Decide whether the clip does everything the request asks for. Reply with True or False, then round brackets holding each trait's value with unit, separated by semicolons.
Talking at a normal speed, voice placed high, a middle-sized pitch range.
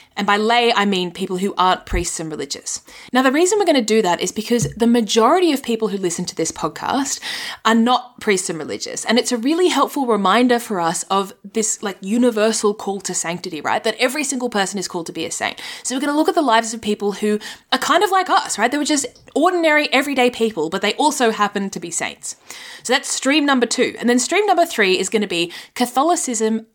False (240 wpm; 225 Hz; 4.8 semitones)